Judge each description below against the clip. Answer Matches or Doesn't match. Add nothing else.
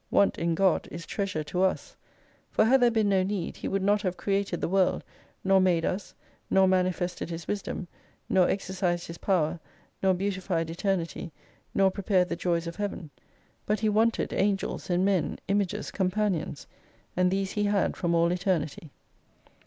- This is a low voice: Doesn't match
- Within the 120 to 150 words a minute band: Doesn't match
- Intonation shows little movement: Matches